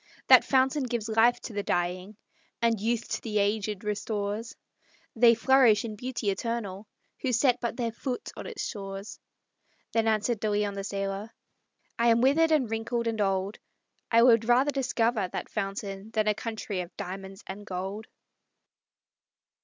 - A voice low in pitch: No, high, 220 Hz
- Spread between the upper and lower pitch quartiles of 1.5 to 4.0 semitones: Yes, average, 2.8 semitones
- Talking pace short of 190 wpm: Yes, average, 160 wpm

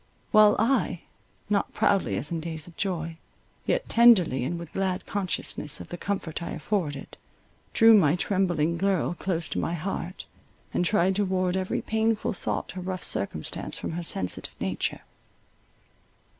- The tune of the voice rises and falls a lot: No, average, 3.4 semitones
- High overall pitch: No, medium, 180 Hz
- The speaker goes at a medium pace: Yes, average, 155 wpm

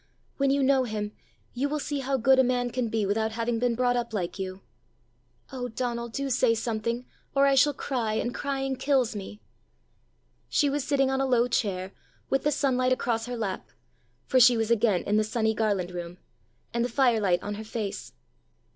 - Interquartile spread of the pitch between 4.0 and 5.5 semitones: No, average, 3.5 semitones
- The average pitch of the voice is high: Yes, high, 240 Hz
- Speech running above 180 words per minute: Yes, average, 195 wpm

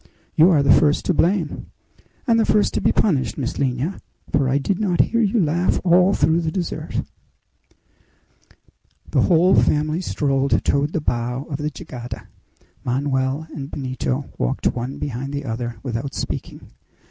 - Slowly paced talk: No, average, 160 wpm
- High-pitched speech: No, medium, 145 Hz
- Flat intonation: No, average, 4.6 semitones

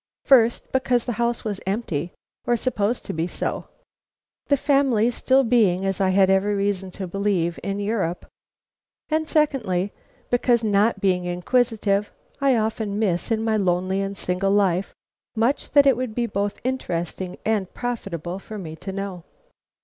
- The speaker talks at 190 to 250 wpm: No, average, 155 wpm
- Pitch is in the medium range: No, high, 205 Hz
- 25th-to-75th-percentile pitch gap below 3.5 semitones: No, average, 4.0 semitones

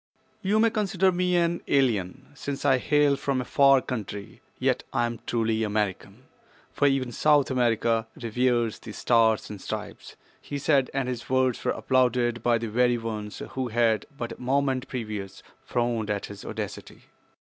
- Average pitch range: Yes, average, 3.3 semitones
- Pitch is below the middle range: Yes, low, 125 Hz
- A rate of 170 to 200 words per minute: No, average, 160 wpm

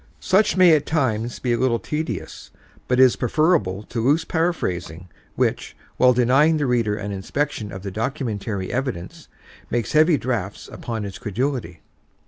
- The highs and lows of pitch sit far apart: Yes, wide, 5.9 semitones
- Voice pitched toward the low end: Yes, low, 120 Hz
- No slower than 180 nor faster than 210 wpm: No, average, 150 wpm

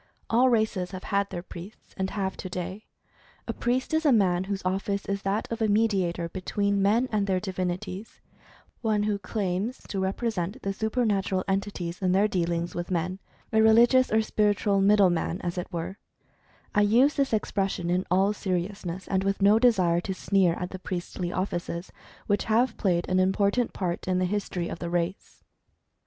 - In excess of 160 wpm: Yes, average, 185 wpm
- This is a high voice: Yes, high, 195 Hz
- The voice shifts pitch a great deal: No, average, 2.7 semitones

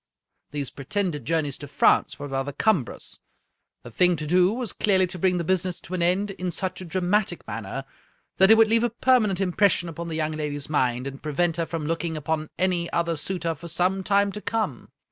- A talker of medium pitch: Yes, medium, 170 Hz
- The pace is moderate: No, fast, 210 wpm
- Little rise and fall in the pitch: No, average, 3.8 semitones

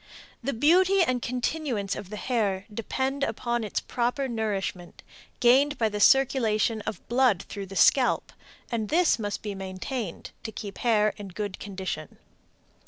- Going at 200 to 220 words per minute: No, average, 155 wpm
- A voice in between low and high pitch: No, high, 225 Hz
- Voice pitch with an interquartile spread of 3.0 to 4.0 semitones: No, average, 4.4 semitones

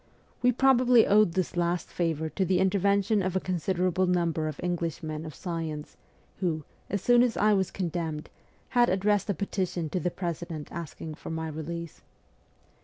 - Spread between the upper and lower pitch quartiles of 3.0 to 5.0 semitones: Yes, average, 3.5 semitones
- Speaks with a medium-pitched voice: Yes, medium, 180 Hz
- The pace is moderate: Yes, average, 170 wpm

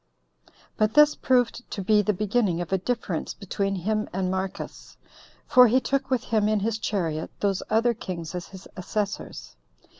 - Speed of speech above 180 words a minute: No, average, 170 wpm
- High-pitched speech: Yes, high, 205 Hz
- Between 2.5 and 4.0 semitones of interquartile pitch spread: Yes, average, 3.5 semitones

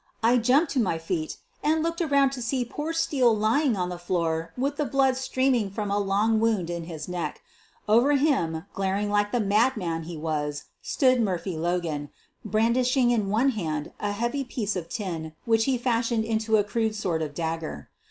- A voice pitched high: Yes, high, 215 Hz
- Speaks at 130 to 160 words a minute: No, average, 190 wpm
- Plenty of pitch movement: Yes, wide, 6.4 semitones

